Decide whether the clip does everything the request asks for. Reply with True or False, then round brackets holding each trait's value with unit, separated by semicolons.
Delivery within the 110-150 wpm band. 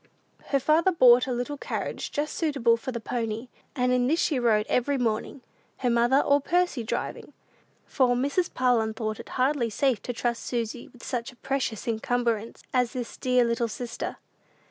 False (175 wpm)